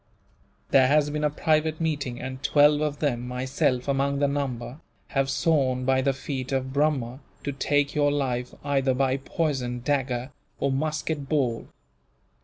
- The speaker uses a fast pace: No, average, 155 wpm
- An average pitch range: No, narrow, 2.2 semitones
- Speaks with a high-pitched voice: No, medium, 140 Hz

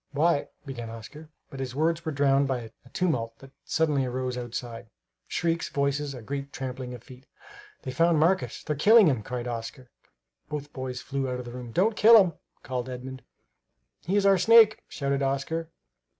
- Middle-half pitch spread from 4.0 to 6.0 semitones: Yes, average, 4.3 semitones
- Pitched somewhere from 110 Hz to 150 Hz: Yes, low, 135 Hz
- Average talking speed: Yes, average, 180 wpm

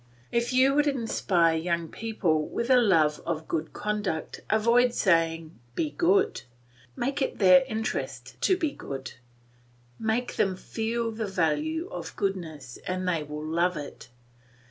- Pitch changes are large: Yes, wide, 6.8 semitones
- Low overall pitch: No, high, 195 Hz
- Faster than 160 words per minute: No, average, 145 wpm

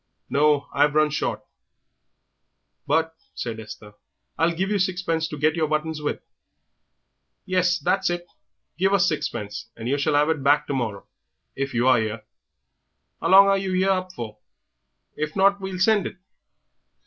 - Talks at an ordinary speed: Yes, average, 160 wpm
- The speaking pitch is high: No, medium, 155 Hz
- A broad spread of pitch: No, average, 4.9 semitones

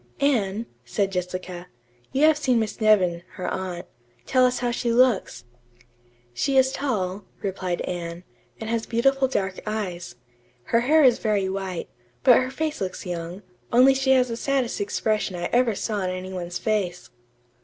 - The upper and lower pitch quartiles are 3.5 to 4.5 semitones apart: No, wide, 5.6 semitones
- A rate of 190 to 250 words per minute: No, average, 165 wpm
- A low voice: No, high, 215 Hz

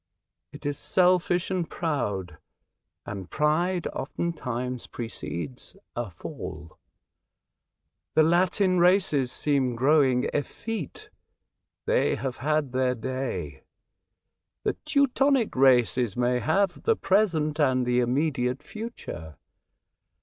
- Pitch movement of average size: No, wide, 6.2 semitones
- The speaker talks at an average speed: No, slow, 100 wpm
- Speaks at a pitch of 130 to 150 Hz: Yes, medium, 140 Hz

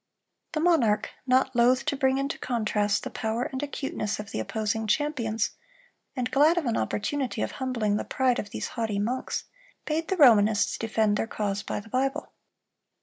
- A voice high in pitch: Yes, high, 240 Hz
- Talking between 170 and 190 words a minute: Yes, average, 175 wpm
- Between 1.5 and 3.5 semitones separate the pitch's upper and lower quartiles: No, average, 4.1 semitones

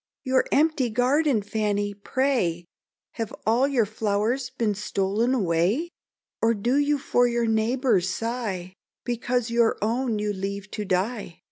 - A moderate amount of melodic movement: Yes, average, 3.7 semitones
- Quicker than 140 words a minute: No, slow, 135 wpm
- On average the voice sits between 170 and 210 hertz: No, high, 225 Hz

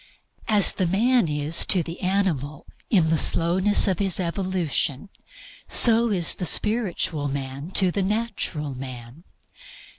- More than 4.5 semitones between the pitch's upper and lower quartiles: Yes, average, 5.1 semitones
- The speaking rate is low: Yes, slow, 130 wpm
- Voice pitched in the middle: Yes, medium, 175 Hz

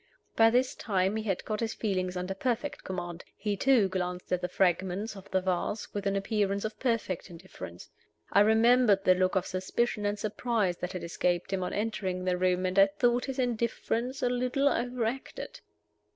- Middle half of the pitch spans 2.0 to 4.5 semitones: Yes, average, 3.9 semitones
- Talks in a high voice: Yes, high, 200 Hz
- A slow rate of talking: No, average, 185 wpm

